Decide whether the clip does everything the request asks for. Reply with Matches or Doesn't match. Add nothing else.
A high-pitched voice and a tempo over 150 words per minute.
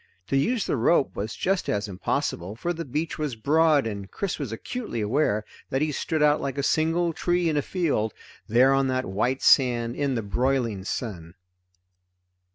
Doesn't match